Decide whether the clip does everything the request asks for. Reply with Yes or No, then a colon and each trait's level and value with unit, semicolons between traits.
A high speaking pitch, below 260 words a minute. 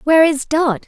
Yes: very high, 295 Hz; fast, 205 wpm